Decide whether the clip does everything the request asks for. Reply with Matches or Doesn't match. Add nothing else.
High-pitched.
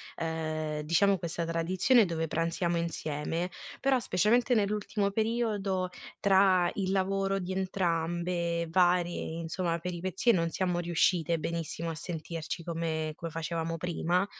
Doesn't match